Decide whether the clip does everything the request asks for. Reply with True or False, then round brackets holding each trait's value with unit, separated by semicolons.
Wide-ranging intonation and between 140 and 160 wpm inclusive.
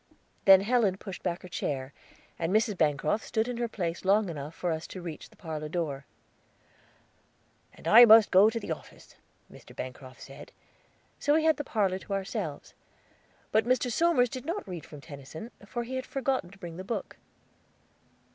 False (6.4 semitones; 180 wpm)